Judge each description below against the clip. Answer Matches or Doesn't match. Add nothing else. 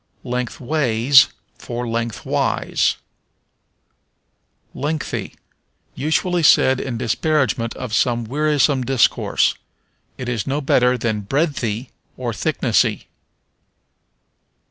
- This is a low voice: Matches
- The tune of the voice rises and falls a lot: Doesn't match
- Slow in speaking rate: Matches